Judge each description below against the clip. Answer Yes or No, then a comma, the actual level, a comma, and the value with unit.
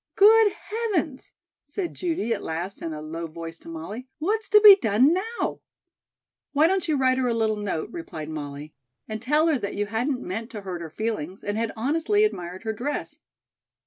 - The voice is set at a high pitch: Yes, high, 230 Hz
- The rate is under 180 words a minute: No, average, 190 wpm